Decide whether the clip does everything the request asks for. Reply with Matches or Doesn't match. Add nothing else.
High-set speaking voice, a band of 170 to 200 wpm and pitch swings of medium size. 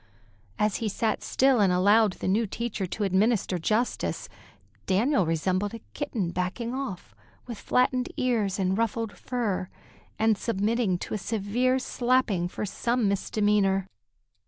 Doesn't match